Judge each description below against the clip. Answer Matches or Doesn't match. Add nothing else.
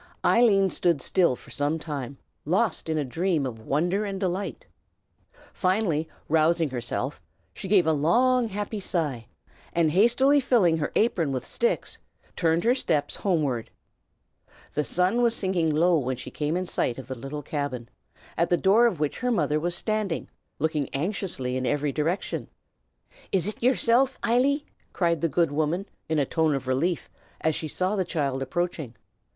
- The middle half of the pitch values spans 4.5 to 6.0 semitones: Matches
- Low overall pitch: Doesn't match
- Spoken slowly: Doesn't match